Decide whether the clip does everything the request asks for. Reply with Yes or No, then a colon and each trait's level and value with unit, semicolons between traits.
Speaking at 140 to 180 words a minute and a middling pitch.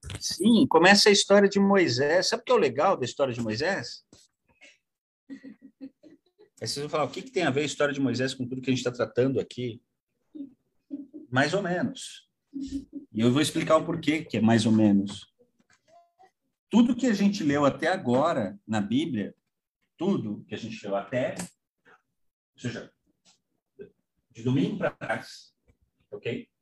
Yes: average, 165 wpm; medium, 165 Hz